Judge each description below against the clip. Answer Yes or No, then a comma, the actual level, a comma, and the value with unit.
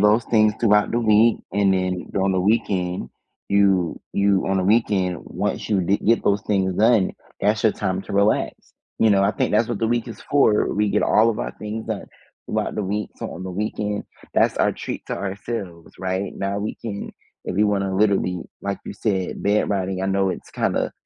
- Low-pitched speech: Yes, low, 100 Hz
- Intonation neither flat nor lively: No, narrow, 2.0 semitones